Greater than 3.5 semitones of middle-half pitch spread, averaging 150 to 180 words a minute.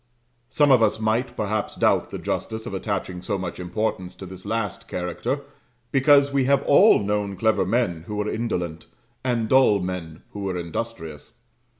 Yes: average, 4.1 semitones; average, 170 wpm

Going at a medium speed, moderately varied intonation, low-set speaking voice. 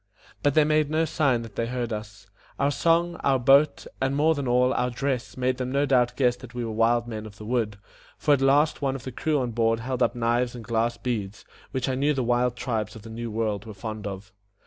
No: fast, 245 wpm; average, 3.2 semitones; low, 125 Hz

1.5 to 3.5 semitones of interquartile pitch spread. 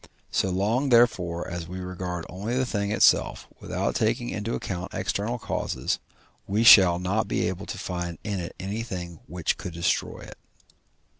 No: average, 3.9 semitones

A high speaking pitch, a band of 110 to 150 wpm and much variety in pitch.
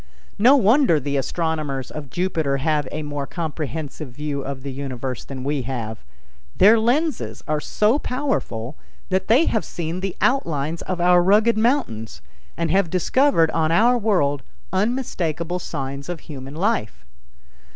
No: medium, 160 Hz; average, 145 wpm; wide, 6.8 semitones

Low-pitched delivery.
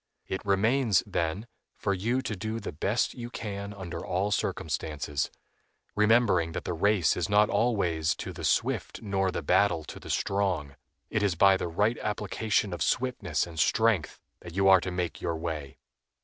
Yes: very low, 95 Hz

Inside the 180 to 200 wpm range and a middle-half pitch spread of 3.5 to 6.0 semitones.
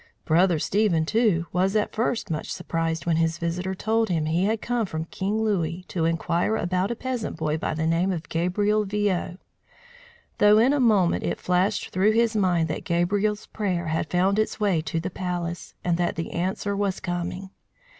Yes: average, 185 wpm; average, 3.8 semitones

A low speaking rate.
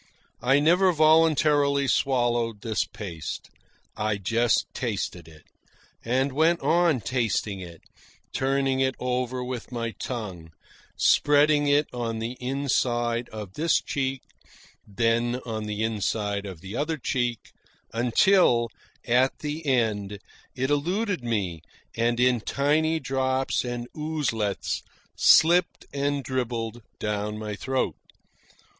Yes: slow, 115 wpm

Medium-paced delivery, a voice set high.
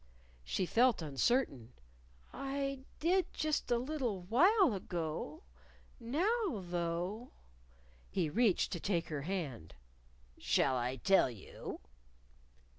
No: slow, 110 wpm; high, 195 Hz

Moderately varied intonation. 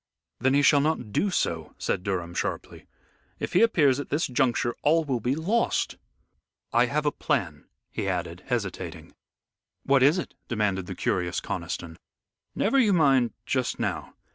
No: wide, 6.9 semitones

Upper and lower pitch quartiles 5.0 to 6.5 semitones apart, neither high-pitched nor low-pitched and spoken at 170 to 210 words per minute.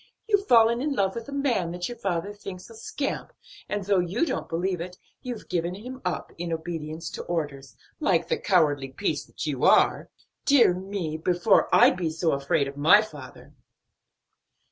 Yes: wide, 5.4 semitones; medium, 180 Hz; average, 185 wpm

